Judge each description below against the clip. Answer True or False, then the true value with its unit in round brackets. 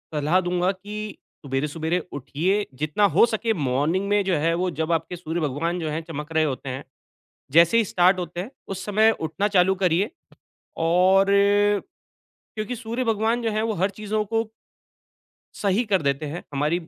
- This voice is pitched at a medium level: True (180 Hz)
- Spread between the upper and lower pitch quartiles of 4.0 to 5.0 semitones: True (4.6 semitones)